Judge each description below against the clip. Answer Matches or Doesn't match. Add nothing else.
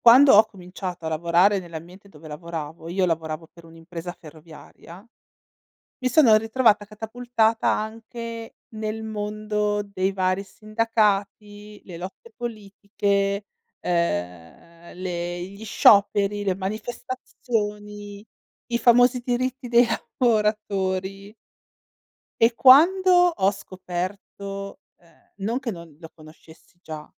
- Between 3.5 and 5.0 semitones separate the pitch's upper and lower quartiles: Matches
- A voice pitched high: Matches